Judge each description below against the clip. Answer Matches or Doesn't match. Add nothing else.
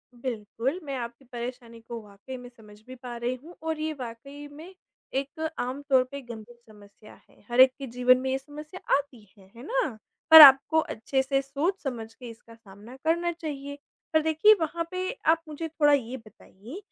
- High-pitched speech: Matches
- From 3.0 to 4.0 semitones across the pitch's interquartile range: Doesn't match